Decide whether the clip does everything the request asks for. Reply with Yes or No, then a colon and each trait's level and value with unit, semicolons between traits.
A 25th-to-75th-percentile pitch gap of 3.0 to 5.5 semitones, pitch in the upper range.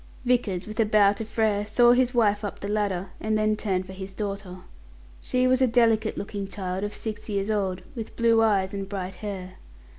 No: narrow, 2.4 semitones; high, 205 Hz